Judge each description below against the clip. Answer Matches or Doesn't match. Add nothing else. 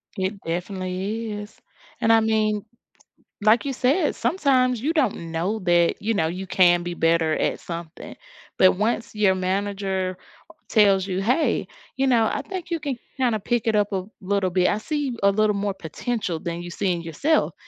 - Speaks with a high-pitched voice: Matches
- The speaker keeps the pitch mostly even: Doesn't match